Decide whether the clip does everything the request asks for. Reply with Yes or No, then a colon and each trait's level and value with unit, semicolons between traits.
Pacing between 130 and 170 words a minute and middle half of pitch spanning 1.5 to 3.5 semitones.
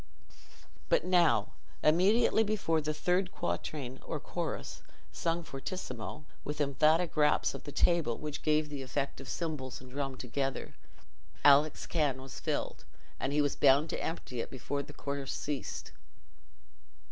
Yes: average, 145 wpm; average, 3.2 semitones